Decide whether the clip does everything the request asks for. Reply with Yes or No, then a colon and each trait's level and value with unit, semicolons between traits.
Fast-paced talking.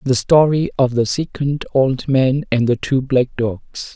No: average, 180 wpm